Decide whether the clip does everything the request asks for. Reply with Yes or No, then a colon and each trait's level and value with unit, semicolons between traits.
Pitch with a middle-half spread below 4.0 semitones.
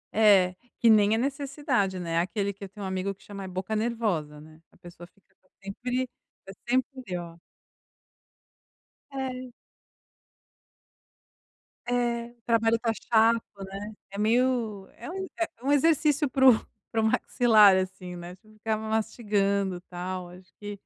No: average, 4.3 semitones